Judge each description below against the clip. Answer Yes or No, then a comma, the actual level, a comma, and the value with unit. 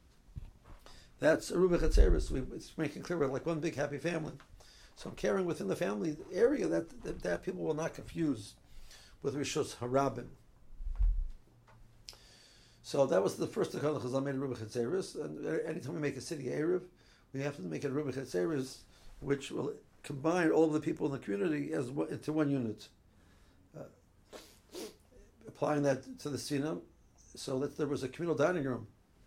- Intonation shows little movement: No, average, 5.0 semitones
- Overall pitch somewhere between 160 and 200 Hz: No, low, 135 Hz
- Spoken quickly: No, average, 160 wpm